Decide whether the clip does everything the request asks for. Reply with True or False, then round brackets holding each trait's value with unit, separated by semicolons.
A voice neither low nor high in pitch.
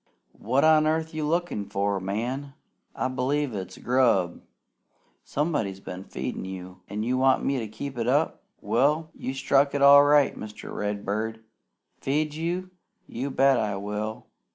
False (130 Hz)